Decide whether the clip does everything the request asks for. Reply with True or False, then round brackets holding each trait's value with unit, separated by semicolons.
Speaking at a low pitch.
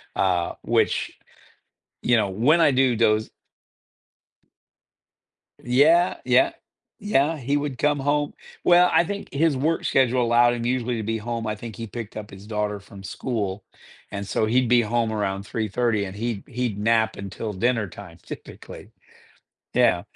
True (115 Hz)